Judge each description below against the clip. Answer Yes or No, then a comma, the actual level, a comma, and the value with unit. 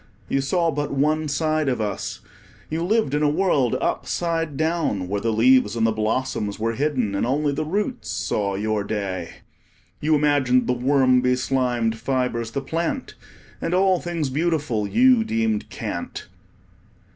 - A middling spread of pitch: No, wide, 5.7 semitones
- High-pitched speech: No, low, 135 Hz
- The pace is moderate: Yes, average, 155 wpm